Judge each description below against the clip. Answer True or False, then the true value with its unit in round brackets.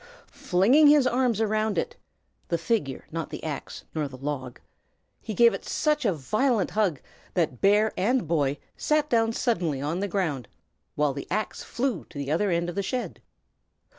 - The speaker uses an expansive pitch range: True (7.4 semitones)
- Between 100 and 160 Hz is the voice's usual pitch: False (195 Hz)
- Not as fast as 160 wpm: False (175 wpm)